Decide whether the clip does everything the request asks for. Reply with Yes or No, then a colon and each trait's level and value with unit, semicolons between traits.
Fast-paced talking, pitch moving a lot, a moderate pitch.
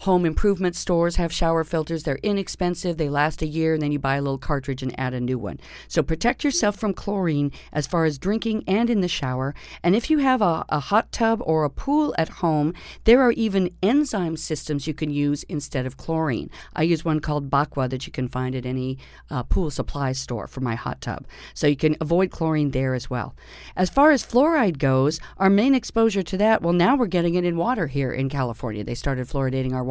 Yes: fast, 225 wpm; wide, 5.7 semitones; medium, 160 Hz